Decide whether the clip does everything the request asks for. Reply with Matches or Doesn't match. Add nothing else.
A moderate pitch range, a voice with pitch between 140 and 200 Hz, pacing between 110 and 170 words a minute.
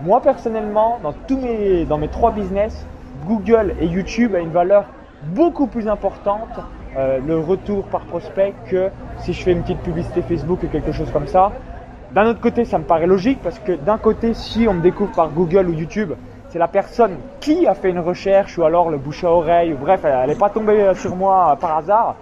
Doesn't match